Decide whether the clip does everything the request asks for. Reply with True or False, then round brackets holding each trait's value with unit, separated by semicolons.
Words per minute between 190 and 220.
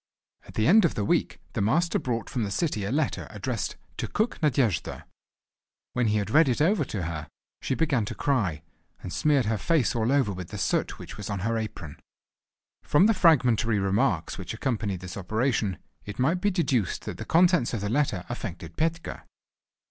True (195 wpm)